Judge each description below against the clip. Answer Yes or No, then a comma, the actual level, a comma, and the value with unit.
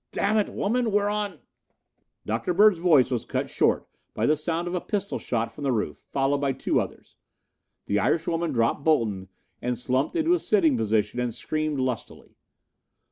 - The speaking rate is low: No, average, 180 wpm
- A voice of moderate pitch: Yes, medium, 150 Hz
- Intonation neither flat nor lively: No, wide, 7.6 semitones